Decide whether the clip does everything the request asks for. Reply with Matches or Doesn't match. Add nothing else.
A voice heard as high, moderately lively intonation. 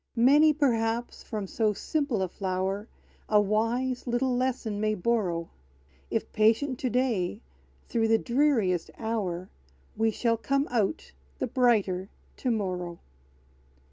Matches